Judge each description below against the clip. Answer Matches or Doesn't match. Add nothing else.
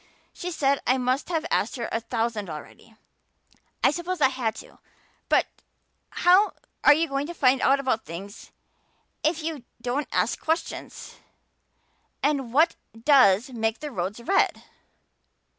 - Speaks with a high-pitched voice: Matches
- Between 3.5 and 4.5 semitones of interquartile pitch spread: Doesn't match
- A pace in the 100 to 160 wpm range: Matches